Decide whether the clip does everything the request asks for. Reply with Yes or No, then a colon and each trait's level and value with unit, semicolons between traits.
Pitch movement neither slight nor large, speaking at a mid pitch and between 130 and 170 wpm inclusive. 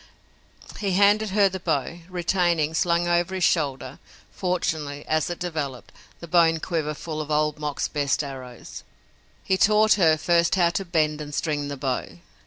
Yes: average, 3.2 semitones; medium, 165 Hz; average, 165 wpm